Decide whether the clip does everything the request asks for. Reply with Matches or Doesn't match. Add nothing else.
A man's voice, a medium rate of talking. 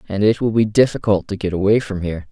Doesn't match